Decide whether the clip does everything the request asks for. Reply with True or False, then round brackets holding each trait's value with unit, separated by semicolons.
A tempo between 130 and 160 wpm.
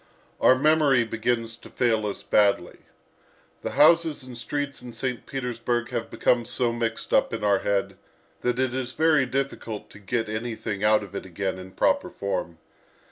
False (170 wpm)